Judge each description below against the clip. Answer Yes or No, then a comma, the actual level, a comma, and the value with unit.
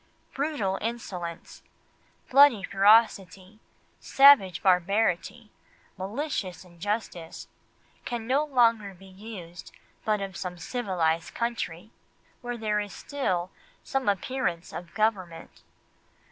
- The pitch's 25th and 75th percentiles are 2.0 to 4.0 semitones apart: No, average, 4.6 semitones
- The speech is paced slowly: Yes, slow, 95 wpm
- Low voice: No, high, 205 Hz